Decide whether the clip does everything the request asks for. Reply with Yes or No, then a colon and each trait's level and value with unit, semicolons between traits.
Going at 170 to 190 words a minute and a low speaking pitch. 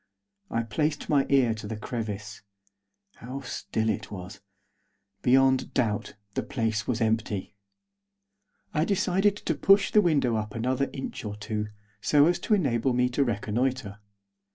No: average, 145 wpm; low, 125 Hz